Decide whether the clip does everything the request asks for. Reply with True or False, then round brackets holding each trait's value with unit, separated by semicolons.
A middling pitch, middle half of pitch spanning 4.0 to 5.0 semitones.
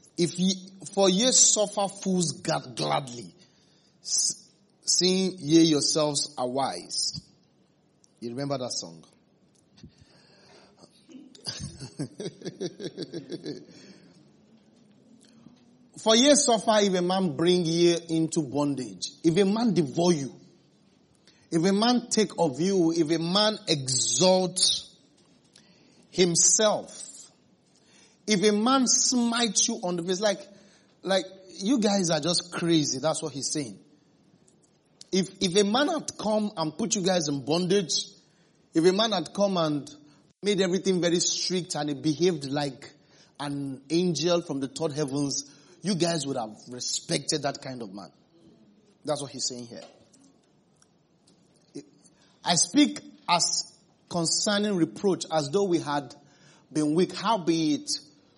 True (175 Hz; 4.6 semitones)